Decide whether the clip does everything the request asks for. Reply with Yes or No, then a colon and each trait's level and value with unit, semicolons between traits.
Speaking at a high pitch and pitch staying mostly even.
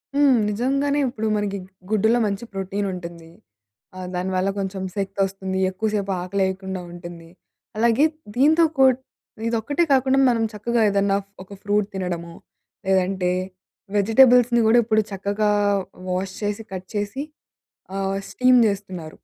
No: high, 200 Hz; average, 3.6 semitones